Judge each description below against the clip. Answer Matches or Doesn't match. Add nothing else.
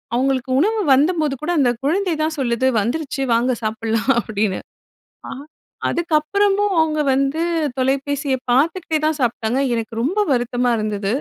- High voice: Matches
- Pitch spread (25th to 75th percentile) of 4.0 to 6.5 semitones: Matches